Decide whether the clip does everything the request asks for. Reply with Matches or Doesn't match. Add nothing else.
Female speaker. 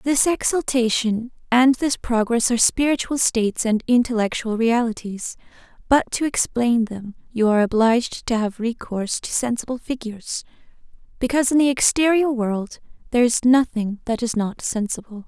Matches